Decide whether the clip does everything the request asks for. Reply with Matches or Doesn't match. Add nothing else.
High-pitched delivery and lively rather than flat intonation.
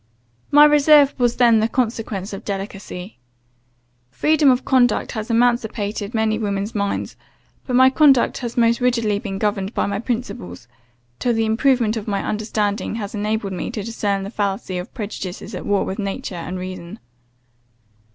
Doesn't match